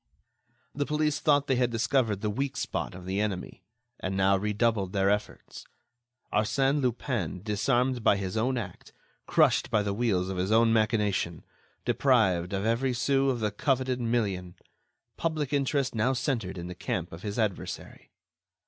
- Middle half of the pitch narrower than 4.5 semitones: No, average, 5.0 semitones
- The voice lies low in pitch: Yes, low, 110 Hz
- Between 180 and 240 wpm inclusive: No, average, 160 wpm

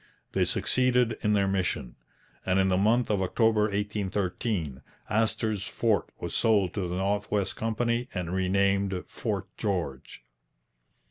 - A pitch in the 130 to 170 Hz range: No, low, 100 Hz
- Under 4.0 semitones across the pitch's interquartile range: Yes, average, 2.8 semitones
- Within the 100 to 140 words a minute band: Yes, slow, 135 wpm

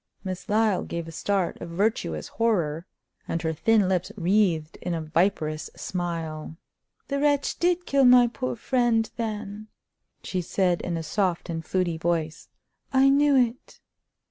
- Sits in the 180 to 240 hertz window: Yes, medium, 185 Hz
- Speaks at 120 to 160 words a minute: Yes, average, 150 wpm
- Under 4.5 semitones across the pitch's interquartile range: No, wide, 5.5 semitones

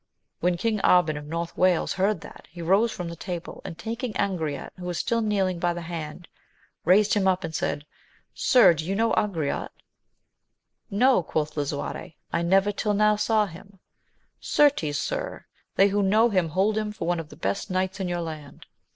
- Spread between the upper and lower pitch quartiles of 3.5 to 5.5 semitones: Yes, average, 4.0 semitones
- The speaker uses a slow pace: No, average, 185 wpm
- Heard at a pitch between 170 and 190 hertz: Yes, medium, 185 Hz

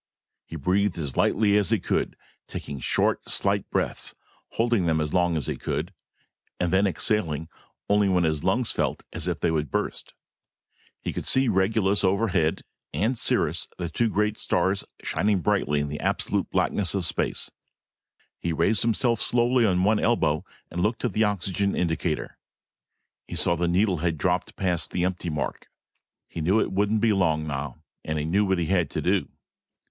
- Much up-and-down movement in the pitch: No, average, 4.2 semitones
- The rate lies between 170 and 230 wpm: Yes, average, 180 wpm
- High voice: No, very low, 95 Hz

